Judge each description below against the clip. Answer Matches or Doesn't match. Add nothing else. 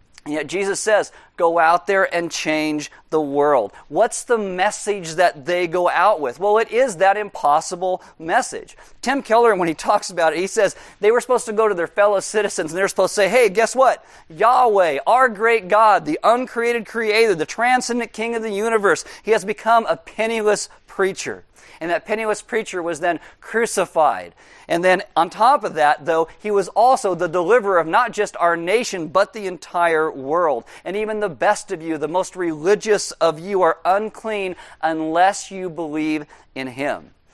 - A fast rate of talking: Doesn't match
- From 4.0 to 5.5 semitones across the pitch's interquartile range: Matches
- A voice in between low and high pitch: Doesn't match